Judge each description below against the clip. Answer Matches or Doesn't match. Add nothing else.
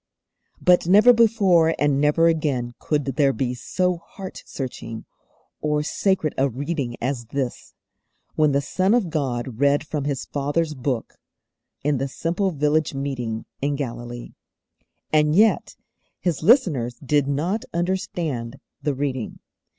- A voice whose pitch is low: Doesn't match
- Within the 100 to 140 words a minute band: Matches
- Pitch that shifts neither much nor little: Matches